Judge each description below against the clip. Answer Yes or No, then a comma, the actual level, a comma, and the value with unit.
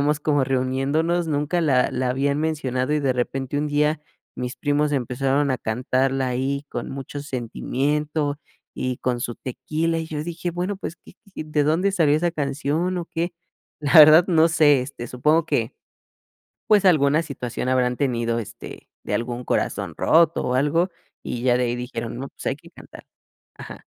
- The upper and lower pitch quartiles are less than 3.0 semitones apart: No, average, 3.6 semitones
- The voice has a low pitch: No, medium, 145 Hz